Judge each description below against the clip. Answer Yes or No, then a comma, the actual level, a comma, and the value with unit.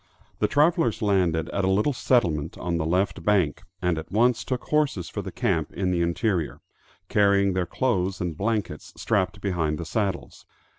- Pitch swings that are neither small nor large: Yes, average, 4.0 semitones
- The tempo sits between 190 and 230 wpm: No, average, 175 wpm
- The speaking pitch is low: Yes, very low, 95 Hz